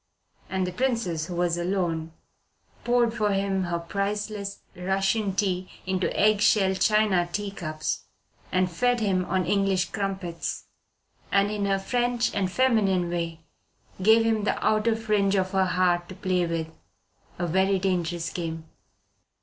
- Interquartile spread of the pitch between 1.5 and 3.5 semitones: Yes, average, 2.8 semitones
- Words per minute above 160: No, average, 145 wpm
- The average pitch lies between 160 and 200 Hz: Yes, high, 190 Hz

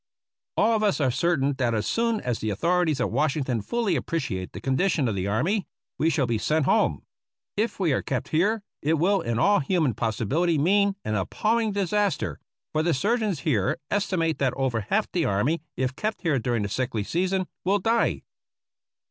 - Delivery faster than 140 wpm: Yes, average, 190 wpm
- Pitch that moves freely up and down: Yes, wide, 7.8 semitones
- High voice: No, medium, 160 Hz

